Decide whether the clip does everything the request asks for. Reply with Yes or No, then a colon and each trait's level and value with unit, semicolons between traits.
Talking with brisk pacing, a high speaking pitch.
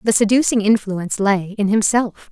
No: average, 155 wpm; high, 210 Hz